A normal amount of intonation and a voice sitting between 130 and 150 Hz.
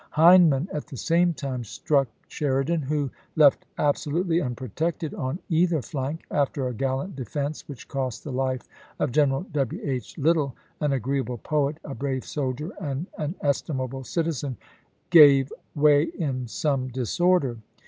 Yes: average, 3.0 semitones; medium, 140 Hz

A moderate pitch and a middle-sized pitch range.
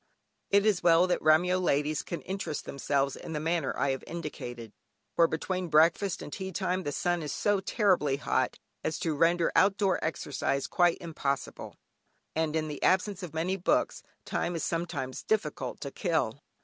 Yes: medium, 165 Hz; average, 3.6 semitones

